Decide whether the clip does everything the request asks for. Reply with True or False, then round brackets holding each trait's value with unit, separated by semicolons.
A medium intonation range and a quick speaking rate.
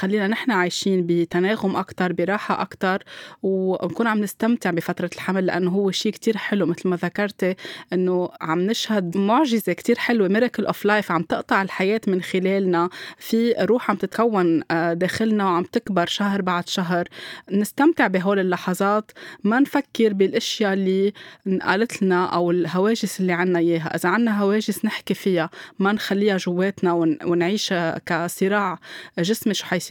True (3.0 semitones; 140 wpm)